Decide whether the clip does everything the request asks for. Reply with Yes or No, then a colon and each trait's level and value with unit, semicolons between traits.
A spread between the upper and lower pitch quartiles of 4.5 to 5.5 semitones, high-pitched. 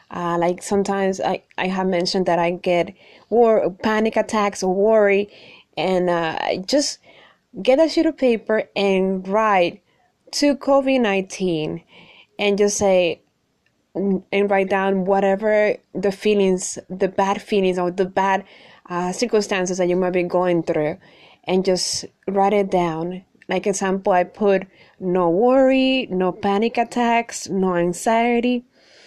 No: average, 2.9 semitones; high, 195 Hz